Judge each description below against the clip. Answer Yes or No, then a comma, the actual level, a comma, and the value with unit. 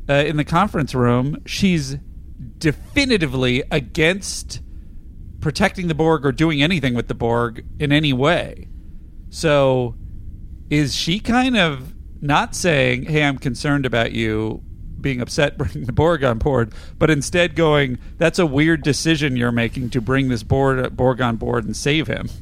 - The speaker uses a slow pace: No, average, 155 wpm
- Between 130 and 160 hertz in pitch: Yes, low, 135 Hz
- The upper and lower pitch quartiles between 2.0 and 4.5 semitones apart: No, average, 4.9 semitones